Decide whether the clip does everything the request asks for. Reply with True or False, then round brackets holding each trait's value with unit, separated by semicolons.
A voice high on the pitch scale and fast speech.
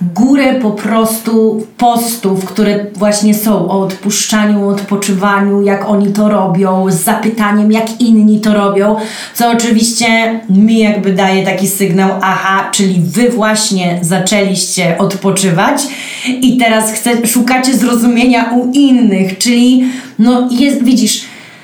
False (215 Hz; 120 wpm)